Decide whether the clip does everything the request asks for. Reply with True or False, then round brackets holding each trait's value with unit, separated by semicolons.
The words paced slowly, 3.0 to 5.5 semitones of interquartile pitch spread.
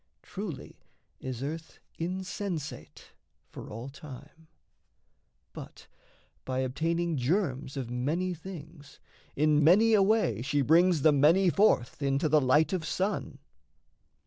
True (120 wpm; 4.9 semitones)